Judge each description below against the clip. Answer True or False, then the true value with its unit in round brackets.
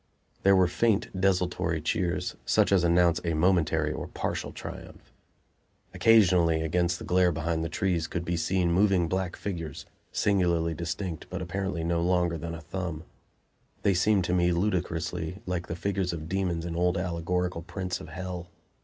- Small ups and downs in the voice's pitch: True (1.8 semitones)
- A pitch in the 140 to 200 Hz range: False (90 Hz)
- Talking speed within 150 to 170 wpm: True (160 wpm)